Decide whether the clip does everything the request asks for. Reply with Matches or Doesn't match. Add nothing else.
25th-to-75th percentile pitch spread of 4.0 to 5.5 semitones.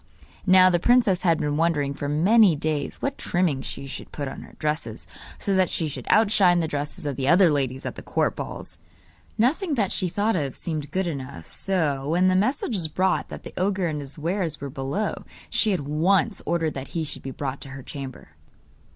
Matches